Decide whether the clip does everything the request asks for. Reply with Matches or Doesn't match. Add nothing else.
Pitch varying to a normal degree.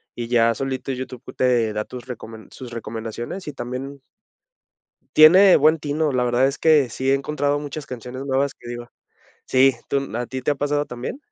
Matches